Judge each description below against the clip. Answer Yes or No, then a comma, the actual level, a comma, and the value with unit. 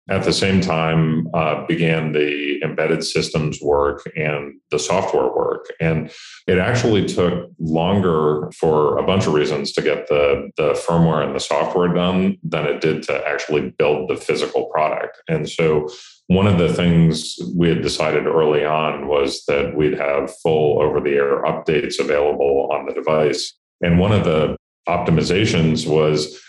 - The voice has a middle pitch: No, very low, 80 Hz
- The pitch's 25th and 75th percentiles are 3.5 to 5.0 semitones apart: Yes, average, 3.8 semitones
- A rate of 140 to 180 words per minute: Yes, average, 165 wpm